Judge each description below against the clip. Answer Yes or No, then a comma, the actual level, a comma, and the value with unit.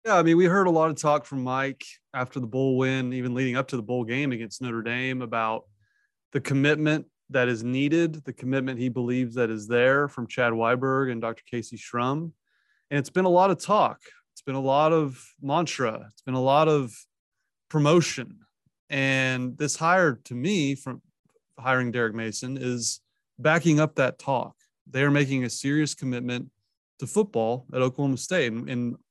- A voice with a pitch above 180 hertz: No, low, 130 Hz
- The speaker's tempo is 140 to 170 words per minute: No, average, 190 wpm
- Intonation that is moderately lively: Yes, average, 3.3 semitones